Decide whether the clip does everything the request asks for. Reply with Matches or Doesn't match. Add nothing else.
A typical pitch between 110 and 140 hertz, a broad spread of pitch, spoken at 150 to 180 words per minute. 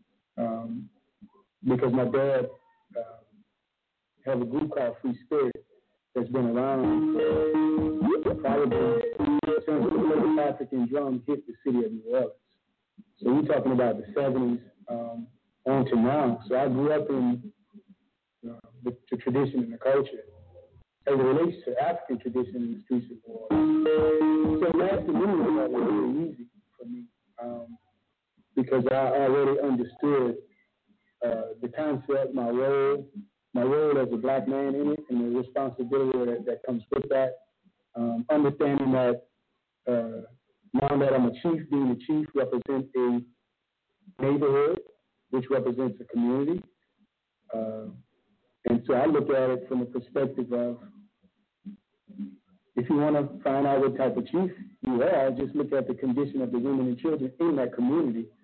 Matches